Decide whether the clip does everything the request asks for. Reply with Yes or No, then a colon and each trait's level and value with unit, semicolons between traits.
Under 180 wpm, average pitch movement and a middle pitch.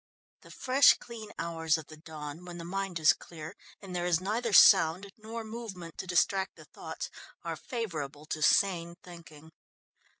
Yes: average, 165 wpm; average, 4.1 semitones; medium, 175 Hz